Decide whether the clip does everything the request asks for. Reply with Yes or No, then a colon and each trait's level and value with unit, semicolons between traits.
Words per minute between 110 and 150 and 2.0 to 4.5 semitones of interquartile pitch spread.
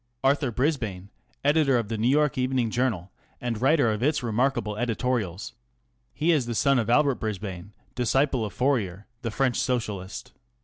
No: average, 160 wpm; average, 4.1 semitones